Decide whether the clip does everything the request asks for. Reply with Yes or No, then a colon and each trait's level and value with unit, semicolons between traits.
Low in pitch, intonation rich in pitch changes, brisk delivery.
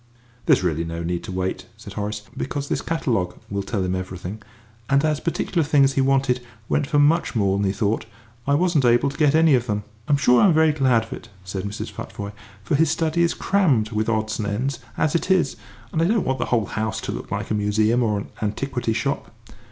Yes: low, 120 Hz; wide, 6.1 semitones; fast, 230 wpm